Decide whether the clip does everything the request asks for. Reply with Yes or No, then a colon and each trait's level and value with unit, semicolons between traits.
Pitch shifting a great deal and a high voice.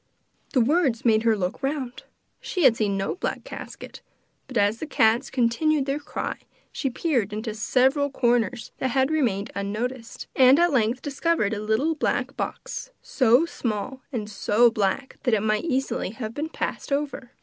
No: average, 4.2 semitones; high, 245 Hz